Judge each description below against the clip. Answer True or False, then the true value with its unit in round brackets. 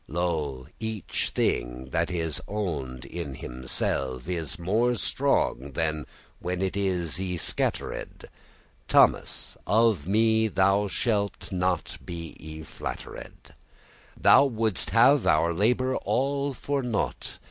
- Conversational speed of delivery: False (125 wpm)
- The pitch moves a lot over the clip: True (6.0 semitones)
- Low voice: True (90 Hz)